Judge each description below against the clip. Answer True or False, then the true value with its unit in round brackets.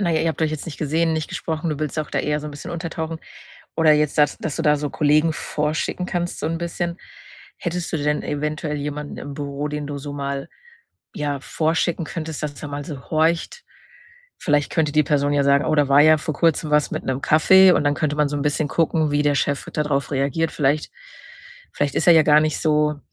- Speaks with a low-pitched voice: False (150 Hz)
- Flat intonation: True (1.7 semitones)